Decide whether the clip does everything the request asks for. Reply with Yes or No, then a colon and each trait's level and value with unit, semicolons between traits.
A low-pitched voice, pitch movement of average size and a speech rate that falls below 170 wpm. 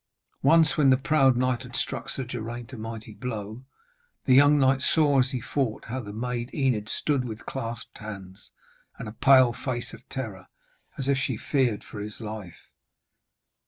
No: low, 125 Hz; average, 3.4 semitones; average, 175 wpm